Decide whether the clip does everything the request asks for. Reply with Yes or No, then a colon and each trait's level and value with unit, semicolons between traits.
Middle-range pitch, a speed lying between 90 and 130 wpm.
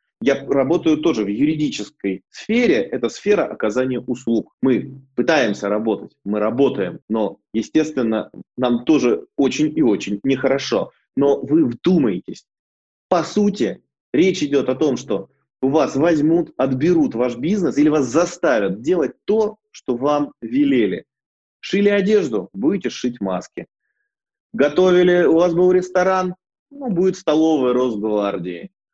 Yes: medium, 155 Hz; average, 125 wpm